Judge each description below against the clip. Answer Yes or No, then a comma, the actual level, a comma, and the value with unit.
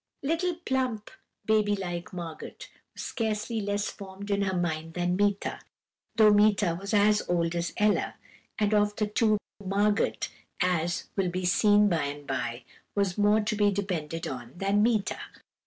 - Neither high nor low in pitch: No, high, 200 Hz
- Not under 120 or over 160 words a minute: Yes, average, 155 wpm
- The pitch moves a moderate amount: Yes, average, 3.1 semitones